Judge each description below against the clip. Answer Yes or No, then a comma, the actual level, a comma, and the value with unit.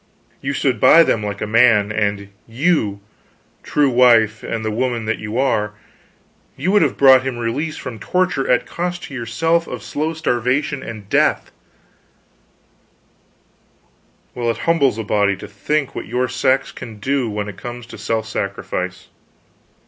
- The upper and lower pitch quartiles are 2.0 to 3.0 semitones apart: No, average, 4.5 semitones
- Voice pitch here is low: Yes, low, 120 Hz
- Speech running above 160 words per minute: No, average, 155 wpm